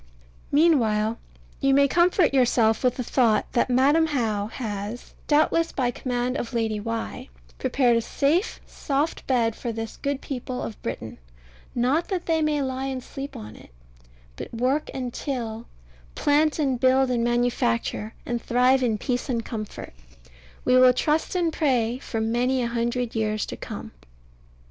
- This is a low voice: No, very high, 250 Hz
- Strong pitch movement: No, average, 3.3 semitones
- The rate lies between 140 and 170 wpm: Yes, average, 160 wpm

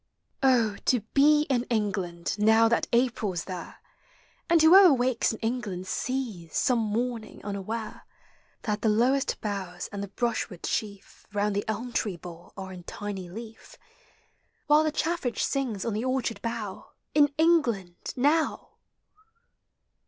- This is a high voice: Yes, high, 225 Hz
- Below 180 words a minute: Yes, average, 140 wpm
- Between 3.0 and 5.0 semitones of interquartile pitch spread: Yes, average, 4.3 semitones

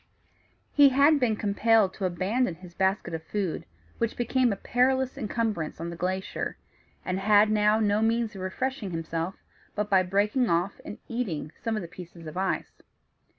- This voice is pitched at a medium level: No, high, 205 Hz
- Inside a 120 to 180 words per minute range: Yes, average, 170 wpm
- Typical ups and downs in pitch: Yes, average, 4.0 semitones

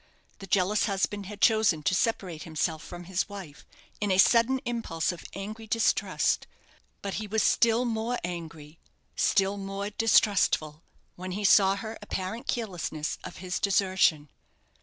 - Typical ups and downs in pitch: Yes, average, 3.7 semitones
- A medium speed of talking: Yes, average, 145 wpm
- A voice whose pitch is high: Yes, high, 195 Hz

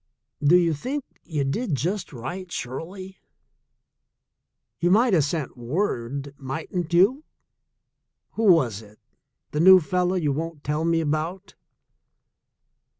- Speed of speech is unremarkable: No, slow, 125 wpm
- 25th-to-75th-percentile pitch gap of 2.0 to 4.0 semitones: No, average, 4.8 semitones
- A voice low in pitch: No, medium, 165 Hz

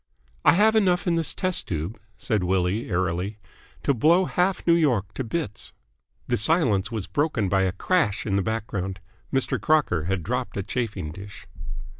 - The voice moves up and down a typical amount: No, wide, 8.6 semitones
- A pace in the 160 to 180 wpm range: Yes, average, 170 wpm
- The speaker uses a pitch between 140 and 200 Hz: No, low, 110 Hz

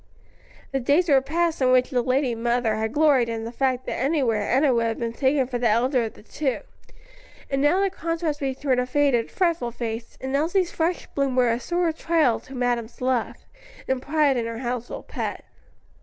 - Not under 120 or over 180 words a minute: No, average, 200 wpm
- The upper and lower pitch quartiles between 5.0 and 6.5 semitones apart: No, average, 3.6 semitones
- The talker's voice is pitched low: No, very high, 260 Hz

